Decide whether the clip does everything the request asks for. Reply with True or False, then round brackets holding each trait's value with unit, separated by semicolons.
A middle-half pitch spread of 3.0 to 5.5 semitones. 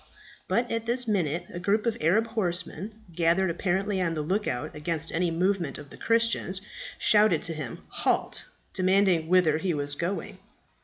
True (4.1 semitones)